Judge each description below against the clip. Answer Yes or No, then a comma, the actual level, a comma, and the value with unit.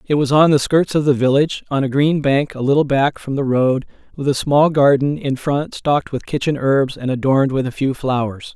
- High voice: No, medium, 140 Hz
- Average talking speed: No, fast, 240 wpm